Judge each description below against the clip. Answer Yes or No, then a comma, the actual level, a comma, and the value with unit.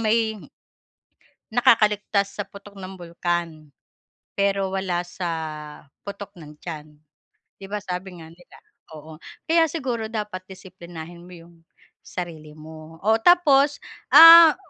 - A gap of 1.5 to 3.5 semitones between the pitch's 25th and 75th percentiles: No, average, 4.2 semitones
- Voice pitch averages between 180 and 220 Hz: Yes, high, 190 Hz